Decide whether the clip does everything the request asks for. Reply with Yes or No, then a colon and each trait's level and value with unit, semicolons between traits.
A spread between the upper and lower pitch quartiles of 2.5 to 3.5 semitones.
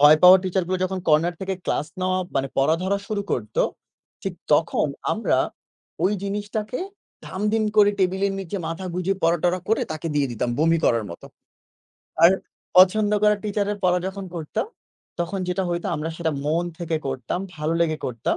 No: average, 3.9 semitones